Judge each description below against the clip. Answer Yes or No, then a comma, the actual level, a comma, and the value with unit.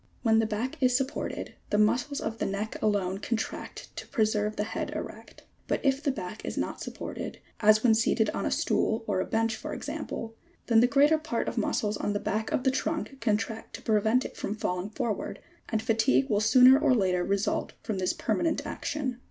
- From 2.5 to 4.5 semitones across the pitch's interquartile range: Yes, average, 3.3 semitones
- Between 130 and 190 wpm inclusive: No, fast, 205 wpm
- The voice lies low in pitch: No, high, 220 Hz